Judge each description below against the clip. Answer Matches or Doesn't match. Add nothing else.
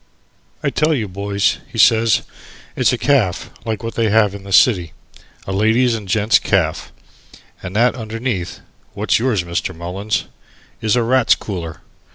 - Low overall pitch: Matches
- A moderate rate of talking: Matches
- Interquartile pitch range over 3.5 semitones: Doesn't match